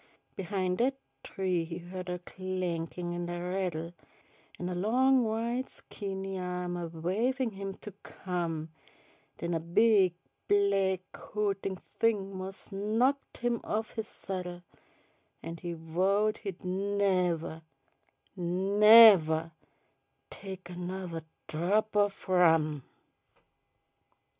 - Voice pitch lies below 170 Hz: No, medium, 185 Hz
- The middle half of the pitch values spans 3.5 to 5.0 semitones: No, average, 2.8 semitones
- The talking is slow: Yes, slow, 110 wpm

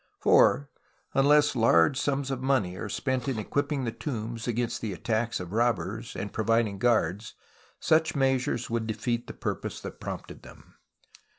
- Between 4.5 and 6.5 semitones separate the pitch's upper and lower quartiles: No, average, 3.5 semitones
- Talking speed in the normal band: Yes, average, 155 wpm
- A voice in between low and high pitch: No, low, 120 Hz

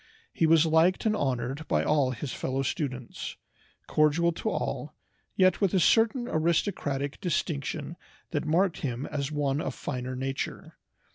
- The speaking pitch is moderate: Yes, medium, 150 Hz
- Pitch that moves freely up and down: No, average, 4.0 semitones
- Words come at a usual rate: Yes, average, 145 wpm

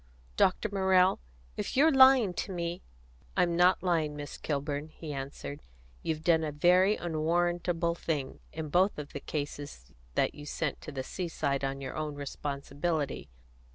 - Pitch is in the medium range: Yes, medium, 155 Hz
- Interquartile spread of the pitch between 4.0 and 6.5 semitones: No, average, 3.6 semitones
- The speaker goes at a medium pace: Yes, average, 160 wpm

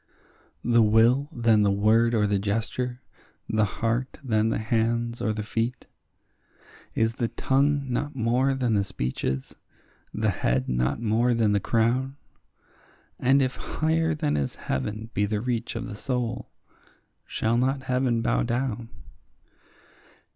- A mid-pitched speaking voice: No, low, 115 Hz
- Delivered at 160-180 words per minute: No, average, 145 wpm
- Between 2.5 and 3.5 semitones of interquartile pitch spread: Yes, average, 2.8 semitones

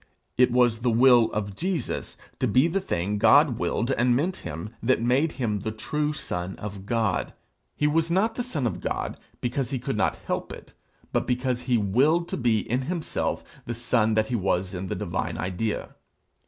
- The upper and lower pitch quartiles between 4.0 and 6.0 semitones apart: Yes, average, 4.4 semitones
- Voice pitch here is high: No, low, 120 Hz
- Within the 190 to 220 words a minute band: Yes, average, 195 wpm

